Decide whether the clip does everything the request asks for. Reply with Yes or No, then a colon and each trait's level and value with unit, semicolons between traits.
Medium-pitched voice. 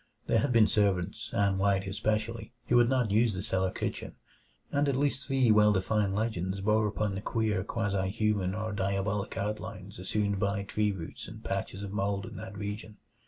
No: low, 105 Hz